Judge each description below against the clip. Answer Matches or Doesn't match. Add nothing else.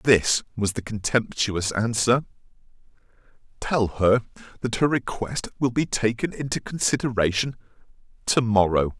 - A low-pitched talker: Matches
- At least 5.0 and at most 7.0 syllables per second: Doesn't match